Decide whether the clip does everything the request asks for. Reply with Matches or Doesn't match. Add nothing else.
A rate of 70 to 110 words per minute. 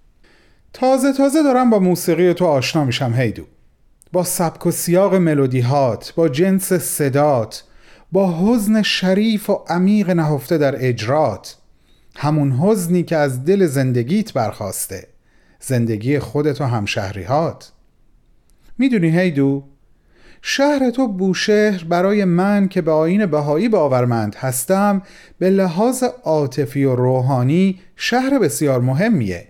Doesn't match